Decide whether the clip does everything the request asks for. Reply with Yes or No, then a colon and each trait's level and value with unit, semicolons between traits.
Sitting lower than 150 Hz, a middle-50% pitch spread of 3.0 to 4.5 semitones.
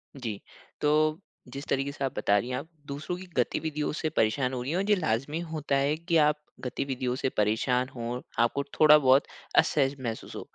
Yes: medium, 140 Hz; average, 3.4 semitones